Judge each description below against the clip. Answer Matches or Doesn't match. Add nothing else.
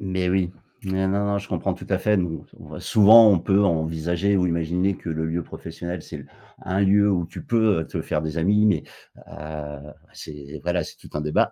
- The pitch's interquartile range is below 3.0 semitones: Doesn't match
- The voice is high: Doesn't match